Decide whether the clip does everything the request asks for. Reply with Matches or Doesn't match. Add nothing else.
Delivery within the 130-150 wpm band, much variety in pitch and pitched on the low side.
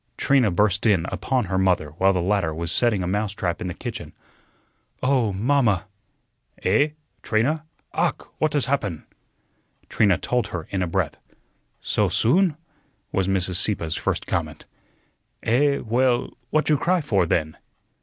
Matches